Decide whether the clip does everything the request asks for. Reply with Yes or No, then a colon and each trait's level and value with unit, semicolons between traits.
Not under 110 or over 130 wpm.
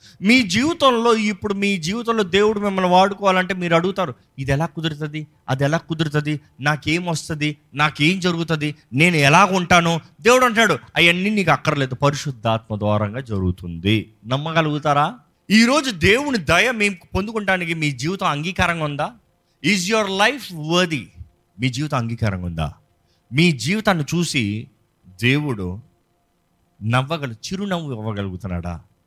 Yes: average, 115 wpm